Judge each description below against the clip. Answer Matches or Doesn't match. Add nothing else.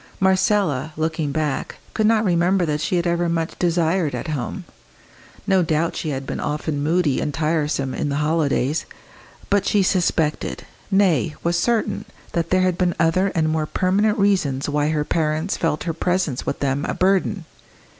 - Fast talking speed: Doesn't match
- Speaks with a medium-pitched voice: Matches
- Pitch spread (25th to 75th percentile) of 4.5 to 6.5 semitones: Doesn't match